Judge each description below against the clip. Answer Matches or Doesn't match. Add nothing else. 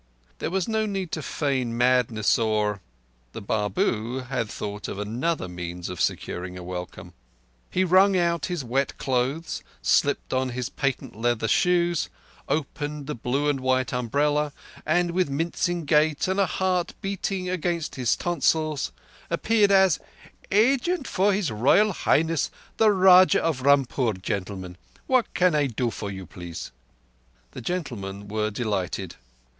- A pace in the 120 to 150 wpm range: Matches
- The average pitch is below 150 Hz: Matches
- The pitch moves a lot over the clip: Matches